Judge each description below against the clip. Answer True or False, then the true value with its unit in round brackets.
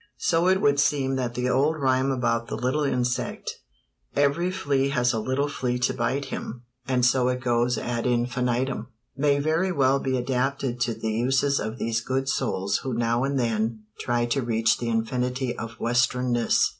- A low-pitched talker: True (125 Hz)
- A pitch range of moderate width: False (2.3 semitones)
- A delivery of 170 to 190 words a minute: True (180 wpm)